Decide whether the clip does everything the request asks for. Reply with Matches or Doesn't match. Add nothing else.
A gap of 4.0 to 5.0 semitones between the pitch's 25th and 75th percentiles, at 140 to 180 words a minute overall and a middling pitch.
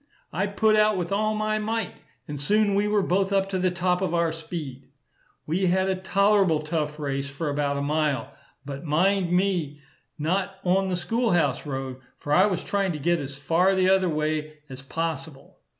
Doesn't match